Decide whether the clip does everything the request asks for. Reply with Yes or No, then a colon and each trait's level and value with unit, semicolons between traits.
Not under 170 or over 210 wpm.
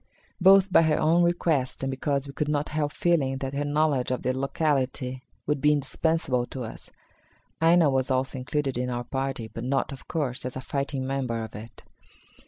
Yes: average, 190 wpm